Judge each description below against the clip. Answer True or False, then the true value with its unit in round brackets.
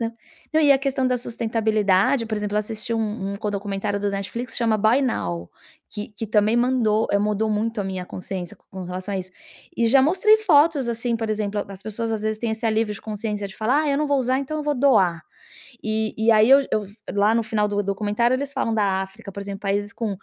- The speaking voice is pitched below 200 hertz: False (220 Hz)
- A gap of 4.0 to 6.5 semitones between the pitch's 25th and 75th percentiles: False (2.9 semitones)